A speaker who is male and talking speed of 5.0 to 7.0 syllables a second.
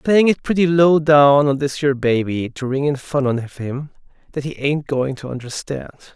Yes: male; 5.4 syllables/s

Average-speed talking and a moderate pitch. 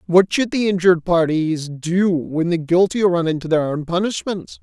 Yes: average, 180 wpm; medium, 175 Hz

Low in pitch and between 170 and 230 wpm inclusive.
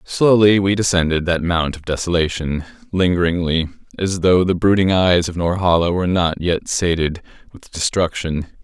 No: very low, 85 Hz; average, 145 wpm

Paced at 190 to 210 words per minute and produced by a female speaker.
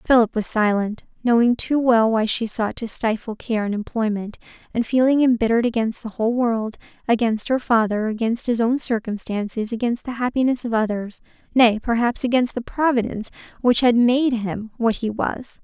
No: average, 175 wpm; female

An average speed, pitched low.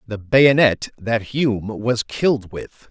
Yes: average, 145 wpm; low, 115 Hz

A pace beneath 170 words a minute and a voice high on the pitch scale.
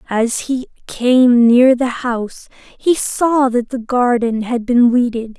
Yes: average, 155 wpm; high, 245 Hz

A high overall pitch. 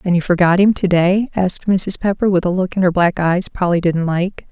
No: medium, 180 Hz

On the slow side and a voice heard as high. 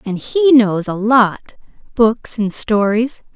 Yes: slow, 125 wpm; high, 225 Hz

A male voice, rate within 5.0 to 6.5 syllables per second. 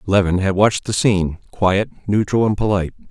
Yes: male; 5.9 syllables/s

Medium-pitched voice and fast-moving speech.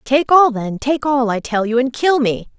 No: very high, 250 Hz; fast, 230 wpm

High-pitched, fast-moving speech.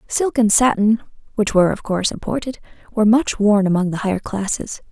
No: high, 210 Hz; average, 185 wpm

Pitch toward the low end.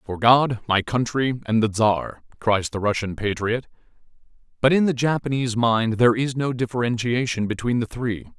Yes: low, 115 Hz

